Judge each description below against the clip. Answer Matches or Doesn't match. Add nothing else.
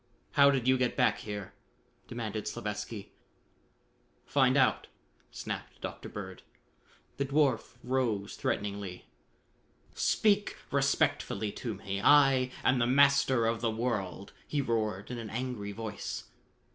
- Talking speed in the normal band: Doesn't match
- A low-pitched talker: Matches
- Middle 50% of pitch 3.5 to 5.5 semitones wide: Matches